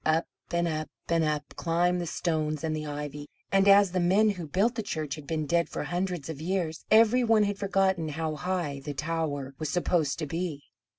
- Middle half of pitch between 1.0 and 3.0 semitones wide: No, average, 3.4 semitones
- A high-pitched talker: No, medium, 165 Hz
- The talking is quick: Yes, fast, 210 wpm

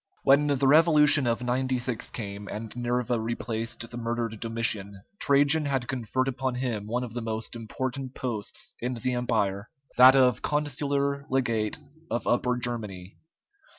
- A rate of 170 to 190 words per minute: No, average, 145 wpm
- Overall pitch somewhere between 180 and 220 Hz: No, low, 120 Hz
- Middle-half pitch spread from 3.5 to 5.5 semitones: No, average, 2.8 semitones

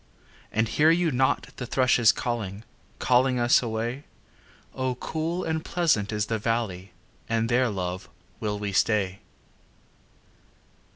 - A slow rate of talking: Yes, slow, 125 wpm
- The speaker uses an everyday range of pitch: Yes, average, 3.7 semitones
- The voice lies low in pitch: Yes, low, 115 Hz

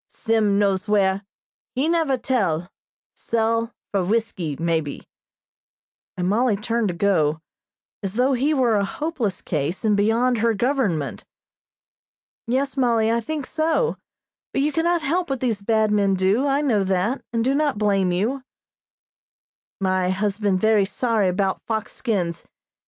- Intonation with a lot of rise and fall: No, average, 5.0 semitones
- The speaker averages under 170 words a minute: Yes, average, 145 wpm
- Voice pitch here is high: Yes, high, 220 Hz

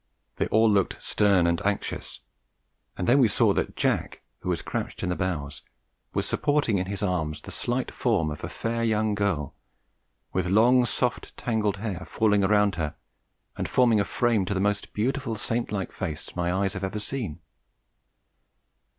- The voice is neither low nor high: No, low, 100 Hz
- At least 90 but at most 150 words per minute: No, average, 175 wpm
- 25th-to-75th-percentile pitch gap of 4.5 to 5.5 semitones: No, average, 3.7 semitones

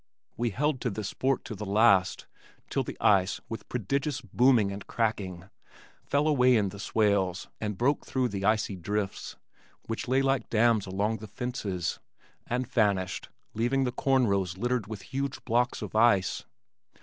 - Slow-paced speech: No, average, 160 wpm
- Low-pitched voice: Yes, low, 110 Hz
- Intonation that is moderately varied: Yes, average, 4.0 semitones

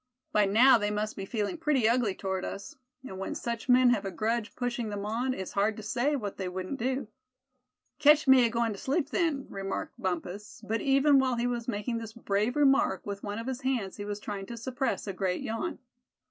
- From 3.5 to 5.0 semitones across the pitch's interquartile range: Yes, average, 4.1 semitones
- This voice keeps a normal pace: No, fast, 215 wpm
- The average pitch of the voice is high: Yes, high, 230 Hz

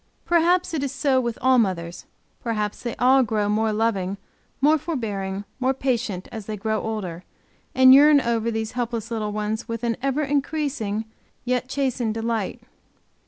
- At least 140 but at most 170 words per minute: Yes, average, 160 wpm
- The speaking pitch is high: Yes, high, 230 Hz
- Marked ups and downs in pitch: No, average, 3.7 semitones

